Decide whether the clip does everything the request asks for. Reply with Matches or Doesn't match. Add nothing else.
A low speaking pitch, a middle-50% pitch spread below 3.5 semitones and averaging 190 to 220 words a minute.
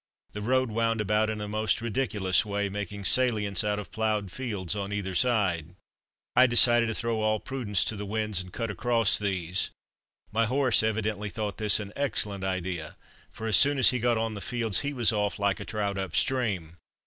Matches